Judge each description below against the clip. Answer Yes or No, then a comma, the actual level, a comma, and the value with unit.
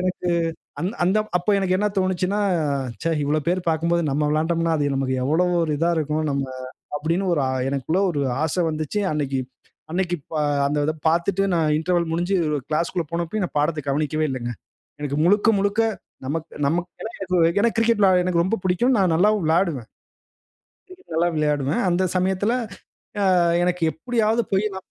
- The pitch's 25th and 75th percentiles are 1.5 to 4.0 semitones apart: Yes, average, 3.5 semitones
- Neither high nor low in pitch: Yes, medium, 170 Hz